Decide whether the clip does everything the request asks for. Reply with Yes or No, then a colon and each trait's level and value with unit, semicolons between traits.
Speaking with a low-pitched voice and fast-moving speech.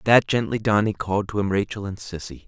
Yes: low, 100 Hz; fast, 240 wpm